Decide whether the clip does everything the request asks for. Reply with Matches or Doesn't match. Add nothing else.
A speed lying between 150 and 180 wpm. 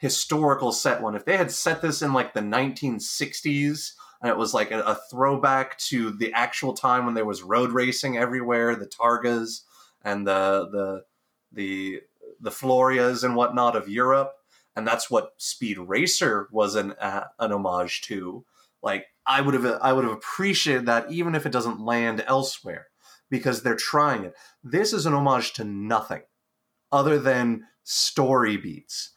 Matches